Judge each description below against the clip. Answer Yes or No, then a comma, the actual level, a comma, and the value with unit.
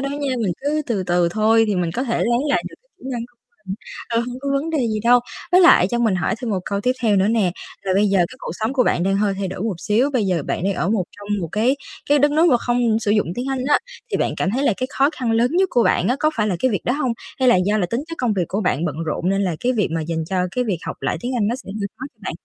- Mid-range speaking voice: No, high, 225 Hz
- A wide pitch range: No, average, 4.8 semitones